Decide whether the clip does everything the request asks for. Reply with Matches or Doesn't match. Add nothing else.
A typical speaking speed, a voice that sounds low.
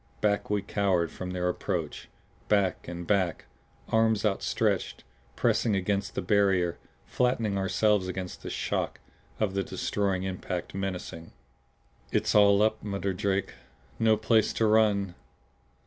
Doesn't match